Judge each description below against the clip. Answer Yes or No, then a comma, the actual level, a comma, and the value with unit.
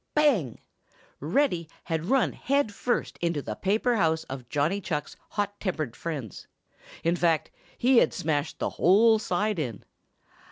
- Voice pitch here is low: No, medium, 170 Hz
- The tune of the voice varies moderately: No, wide, 6.0 semitones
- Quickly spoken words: No, average, 145 wpm